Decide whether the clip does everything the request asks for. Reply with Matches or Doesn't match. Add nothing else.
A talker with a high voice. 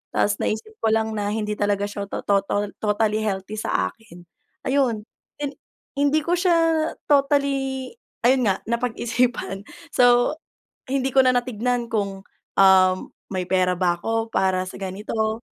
Matches